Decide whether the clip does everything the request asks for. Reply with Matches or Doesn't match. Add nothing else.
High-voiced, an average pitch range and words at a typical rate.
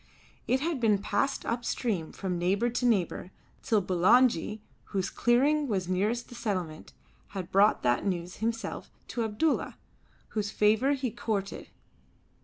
Matches